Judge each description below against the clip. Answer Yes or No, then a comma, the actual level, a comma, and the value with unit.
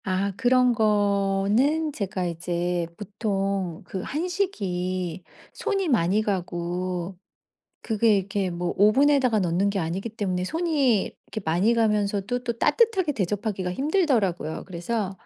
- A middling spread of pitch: Yes, average, 4.8 semitones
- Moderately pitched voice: No, high, 200 Hz